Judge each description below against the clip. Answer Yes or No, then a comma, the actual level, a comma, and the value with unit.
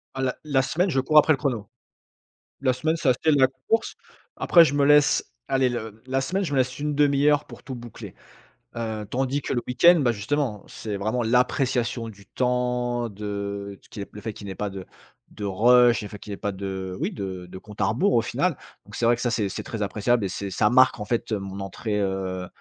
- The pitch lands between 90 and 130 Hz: Yes, low, 120 Hz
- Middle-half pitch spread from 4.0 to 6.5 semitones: Yes, average, 4.7 semitones